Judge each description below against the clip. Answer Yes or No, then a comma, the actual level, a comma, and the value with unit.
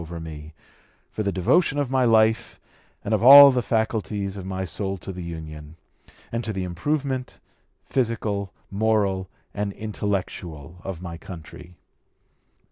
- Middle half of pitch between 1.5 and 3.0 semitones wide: No, average, 4.2 semitones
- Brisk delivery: No, average, 145 wpm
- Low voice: Yes, low, 100 Hz